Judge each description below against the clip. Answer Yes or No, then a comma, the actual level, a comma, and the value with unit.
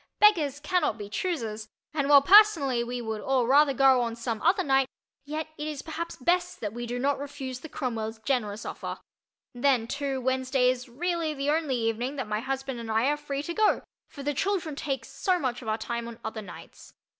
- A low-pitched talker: No, very high, 270 Hz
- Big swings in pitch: No, average, 4.1 semitones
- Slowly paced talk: No, fast, 205 wpm